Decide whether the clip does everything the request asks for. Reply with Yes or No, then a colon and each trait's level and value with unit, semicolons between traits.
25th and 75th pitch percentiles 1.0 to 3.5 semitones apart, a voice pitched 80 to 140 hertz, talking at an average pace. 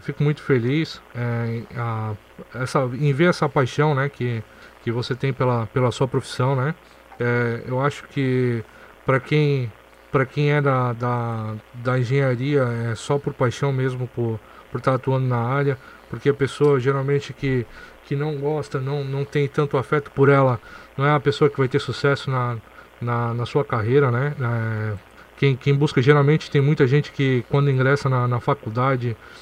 Yes: average, 2.8 semitones; low, 135 Hz; average, 175 wpm